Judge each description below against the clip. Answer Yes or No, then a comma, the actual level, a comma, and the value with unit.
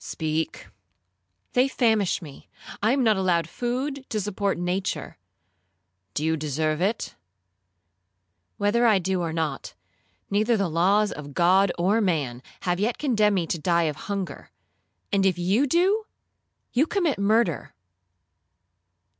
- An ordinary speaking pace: No, slow, 120 wpm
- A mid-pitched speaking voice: Yes, medium, 175 Hz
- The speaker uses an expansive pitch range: Yes, wide, 8.8 semitones